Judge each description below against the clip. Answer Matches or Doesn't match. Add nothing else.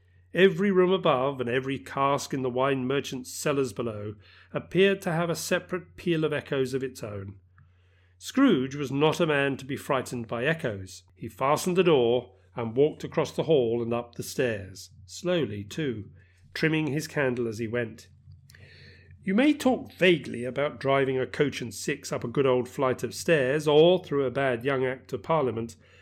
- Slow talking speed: Doesn't match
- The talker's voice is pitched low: Matches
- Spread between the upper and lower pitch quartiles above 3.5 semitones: Matches